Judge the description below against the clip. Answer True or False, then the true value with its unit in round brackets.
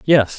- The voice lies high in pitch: False (130 Hz)